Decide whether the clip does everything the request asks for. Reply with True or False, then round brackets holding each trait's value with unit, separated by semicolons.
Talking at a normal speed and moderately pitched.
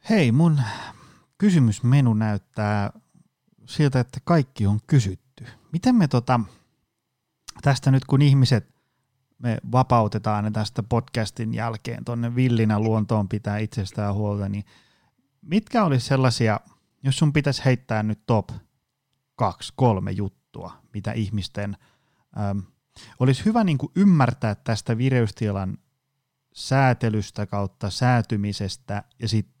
False (110 wpm; 120 Hz)